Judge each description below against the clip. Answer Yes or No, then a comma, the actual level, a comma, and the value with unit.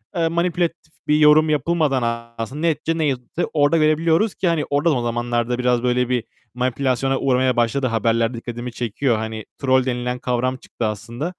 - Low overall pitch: Yes, low, 130 Hz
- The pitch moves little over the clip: No, average, 4.3 semitones